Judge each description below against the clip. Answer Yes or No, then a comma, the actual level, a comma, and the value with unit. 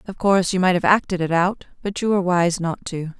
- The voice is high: No, medium, 180 Hz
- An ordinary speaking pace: No, fast, 265 wpm